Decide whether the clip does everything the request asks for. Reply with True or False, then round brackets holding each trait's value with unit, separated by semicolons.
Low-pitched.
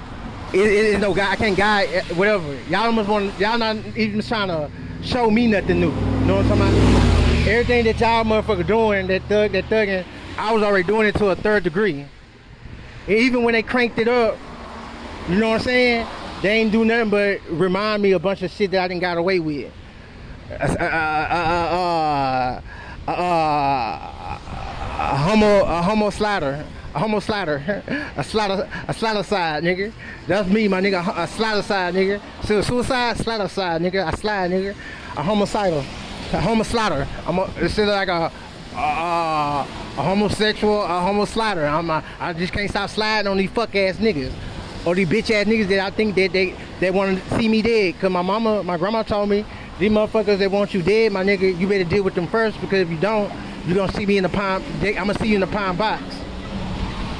False (195 Hz)